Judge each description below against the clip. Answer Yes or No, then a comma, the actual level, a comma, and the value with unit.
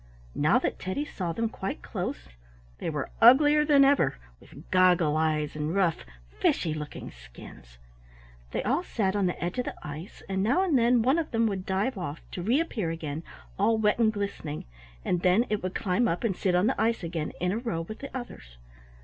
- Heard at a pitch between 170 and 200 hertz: Yes, high, 190 Hz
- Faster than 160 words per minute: Yes, average, 200 wpm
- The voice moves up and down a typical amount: No, wide, 6.1 semitones